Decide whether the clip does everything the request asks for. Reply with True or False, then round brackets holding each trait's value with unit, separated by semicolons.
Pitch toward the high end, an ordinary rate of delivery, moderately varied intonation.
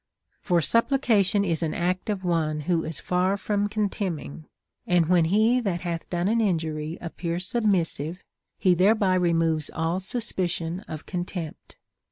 False (180 Hz; 155 wpm; 3.4 semitones)